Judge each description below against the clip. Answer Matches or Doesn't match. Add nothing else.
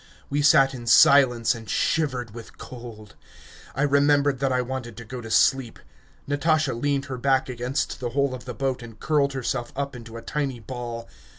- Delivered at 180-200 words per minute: Matches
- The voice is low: Matches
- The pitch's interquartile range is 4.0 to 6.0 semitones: Doesn't match